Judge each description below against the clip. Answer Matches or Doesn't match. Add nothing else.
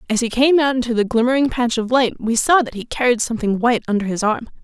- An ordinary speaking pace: Doesn't match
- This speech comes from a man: Doesn't match